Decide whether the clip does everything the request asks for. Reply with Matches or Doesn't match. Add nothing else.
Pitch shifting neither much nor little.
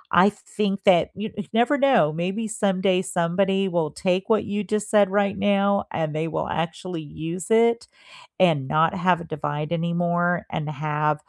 Matches